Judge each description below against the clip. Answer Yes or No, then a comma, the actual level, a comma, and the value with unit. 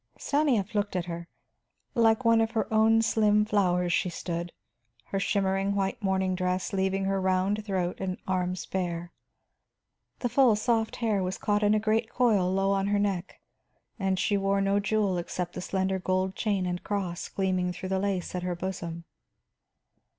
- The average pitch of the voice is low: No, high, 195 Hz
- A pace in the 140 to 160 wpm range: No, average, 170 wpm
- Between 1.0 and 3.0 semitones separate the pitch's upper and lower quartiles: Yes, narrow, 2.4 semitones